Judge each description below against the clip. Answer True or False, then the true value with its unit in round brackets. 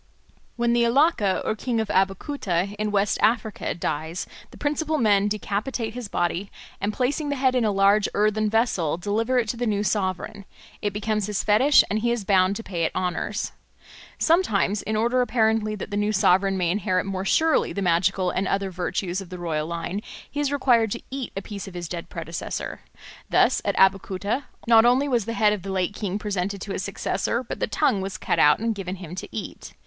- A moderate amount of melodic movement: True (3.4 semitones)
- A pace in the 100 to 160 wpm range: False (205 wpm)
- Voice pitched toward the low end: False (205 Hz)